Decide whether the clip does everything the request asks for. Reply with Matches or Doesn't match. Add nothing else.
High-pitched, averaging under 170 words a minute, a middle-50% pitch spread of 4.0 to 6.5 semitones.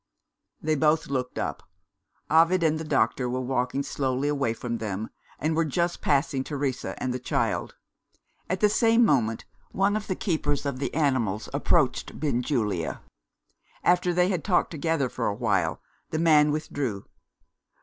Doesn't match